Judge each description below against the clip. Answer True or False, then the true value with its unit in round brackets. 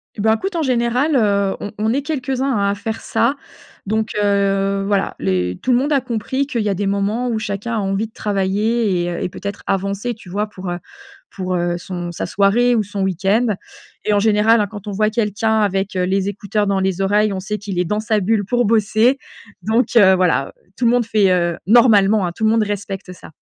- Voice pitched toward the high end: True (205 Hz)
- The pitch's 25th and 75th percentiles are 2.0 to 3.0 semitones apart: True (2.7 semitones)